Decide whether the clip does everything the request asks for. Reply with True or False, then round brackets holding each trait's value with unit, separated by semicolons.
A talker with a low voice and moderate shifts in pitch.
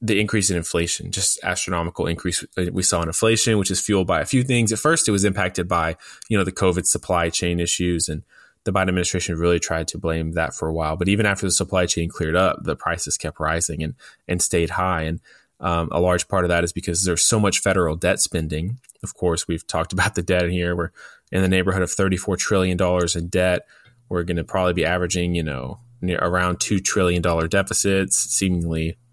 False (90 Hz; 2.3 semitones)